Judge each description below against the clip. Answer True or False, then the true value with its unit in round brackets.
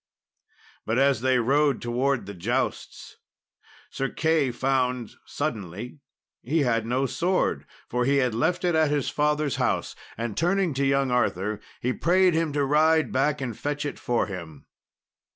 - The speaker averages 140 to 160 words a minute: True (155 wpm)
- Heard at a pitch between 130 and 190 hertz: True (135 Hz)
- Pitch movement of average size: True (3.9 semitones)